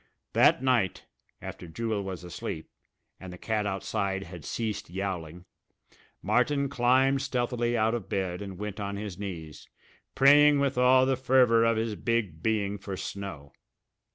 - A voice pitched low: Yes, low, 105 Hz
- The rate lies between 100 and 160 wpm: Yes, average, 150 wpm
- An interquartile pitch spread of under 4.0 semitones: No, average, 4.4 semitones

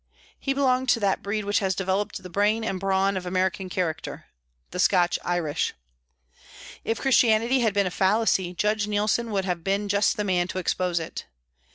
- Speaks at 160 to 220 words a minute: Yes, average, 180 wpm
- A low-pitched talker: No, high, 195 Hz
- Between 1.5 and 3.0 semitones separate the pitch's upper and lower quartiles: Yes, average, 2.7 semitones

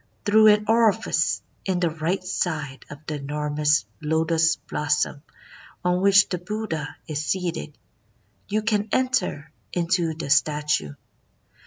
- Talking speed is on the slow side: Yes, slow, 125 wpm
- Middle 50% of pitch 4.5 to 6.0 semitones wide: Yes, average, 4.8 semitones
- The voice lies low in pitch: No, medium, 165 Hz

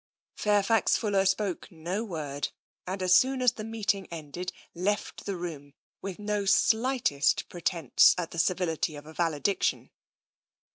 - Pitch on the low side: No, medium, 185 Hz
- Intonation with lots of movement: No, average, 4.1 semitones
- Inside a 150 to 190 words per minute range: No, average, 140 wpm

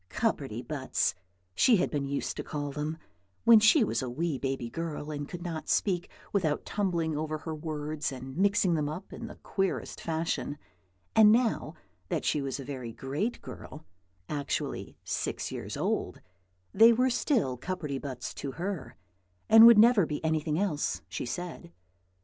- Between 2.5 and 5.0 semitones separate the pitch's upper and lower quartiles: No, wide, 5.5 semitones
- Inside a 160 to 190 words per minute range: Yes, average, 165 wpm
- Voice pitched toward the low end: No, medium, 155 Hz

